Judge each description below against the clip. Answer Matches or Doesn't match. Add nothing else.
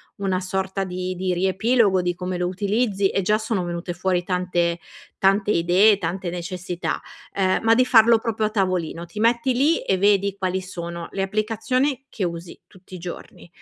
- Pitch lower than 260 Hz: Matches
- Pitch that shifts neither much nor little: Matches